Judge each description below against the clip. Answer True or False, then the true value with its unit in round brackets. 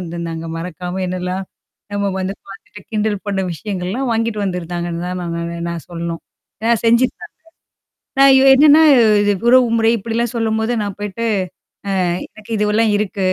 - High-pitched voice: True (205 Hz)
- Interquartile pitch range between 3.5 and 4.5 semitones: True (4.1 semitones)